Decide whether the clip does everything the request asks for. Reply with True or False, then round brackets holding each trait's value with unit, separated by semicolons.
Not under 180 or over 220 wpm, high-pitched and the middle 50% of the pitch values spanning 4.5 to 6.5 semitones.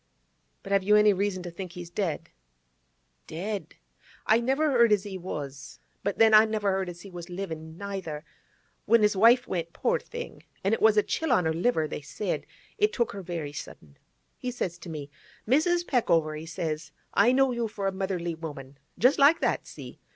True (185 wpm; 195 Hz; 5.3 semitones)